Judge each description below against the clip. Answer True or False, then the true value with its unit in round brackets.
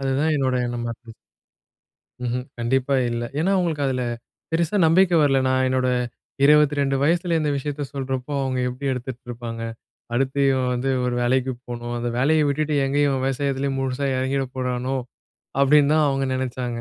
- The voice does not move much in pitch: True (2.3 semitones)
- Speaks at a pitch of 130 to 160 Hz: True (135 Hz)